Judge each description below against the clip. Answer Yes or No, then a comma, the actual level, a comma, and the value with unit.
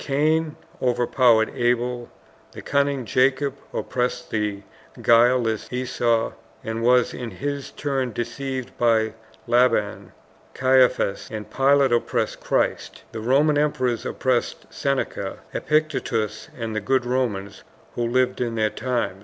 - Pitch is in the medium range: No, low, 125 Hz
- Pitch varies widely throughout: No, narrow, 2.6 semitones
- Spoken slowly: Yes, slow, 120 wpm